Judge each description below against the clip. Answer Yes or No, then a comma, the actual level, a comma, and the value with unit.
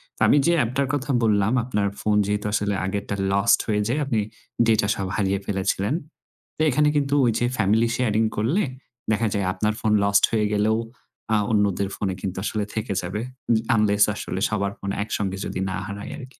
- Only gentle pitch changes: Yes, narrow, 2.3 semitones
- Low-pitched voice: Yes, low, 105 Hz